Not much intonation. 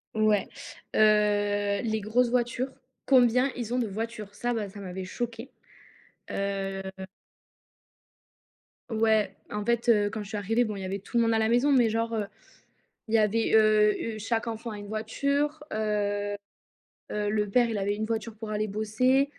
Yes: narrow, 2.2 semitones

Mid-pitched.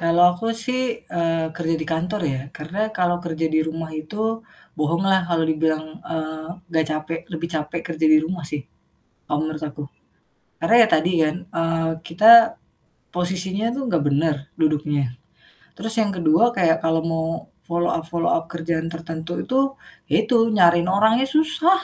Yes: medium, 165 Hz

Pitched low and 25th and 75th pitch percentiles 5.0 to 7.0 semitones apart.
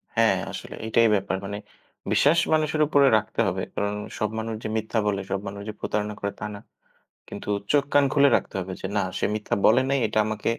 Yes: low, 110 Hz; wide, 5.4 semitones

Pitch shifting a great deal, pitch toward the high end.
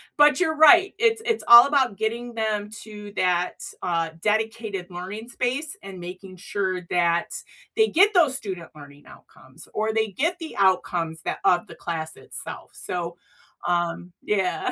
Yes: wide, 6.2 semitones; high, 205 Hz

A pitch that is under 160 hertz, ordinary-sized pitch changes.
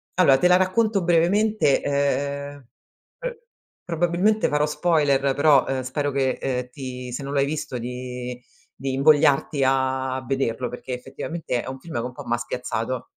Yes: medium, 140 Hz; average, 3.8 semitones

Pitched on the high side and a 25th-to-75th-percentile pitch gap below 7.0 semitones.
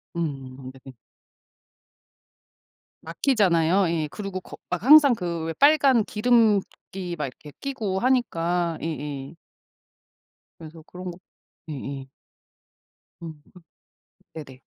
No: medium, 170 Hz; wide, 5.4 semitones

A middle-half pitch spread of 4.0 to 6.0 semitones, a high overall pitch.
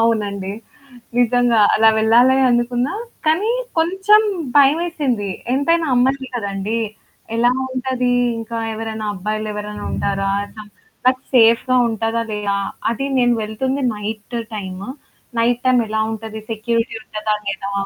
No: average, 3.2 semitones; high, 230 Hz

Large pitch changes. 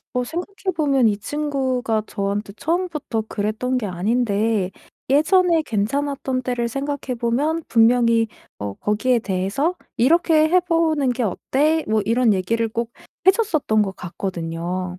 Yes: wide, 6.2 semitones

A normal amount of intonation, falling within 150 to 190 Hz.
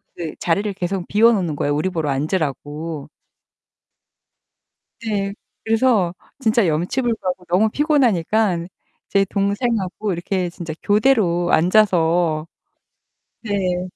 Yes: average, 4.2 semitones; medium, 185 Hz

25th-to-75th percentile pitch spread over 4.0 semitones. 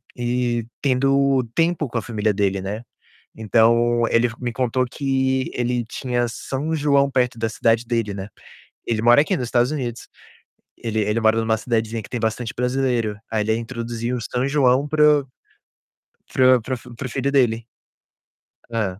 No: average, 2.7 semitones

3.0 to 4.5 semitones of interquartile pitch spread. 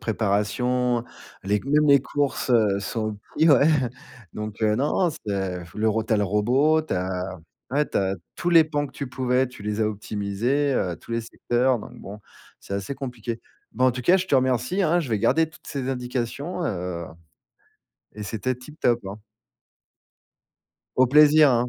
No: average, 5.2 semitones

